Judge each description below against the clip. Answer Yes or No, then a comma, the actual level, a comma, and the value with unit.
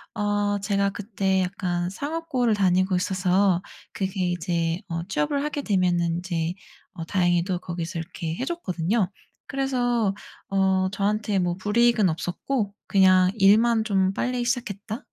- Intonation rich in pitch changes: No, average, 3.4 semitones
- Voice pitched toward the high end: Yes, high, 195 Hz